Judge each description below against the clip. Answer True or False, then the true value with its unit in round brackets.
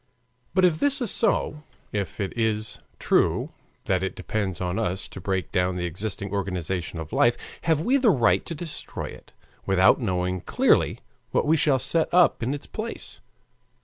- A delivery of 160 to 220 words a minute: True (175 wpm)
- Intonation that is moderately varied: False (8.9 semitones)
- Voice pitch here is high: False (105 Hz)